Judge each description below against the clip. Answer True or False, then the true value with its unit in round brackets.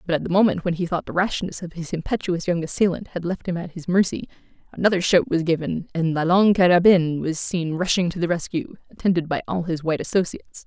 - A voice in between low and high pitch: True (175 Hz)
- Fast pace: True (225 wpm)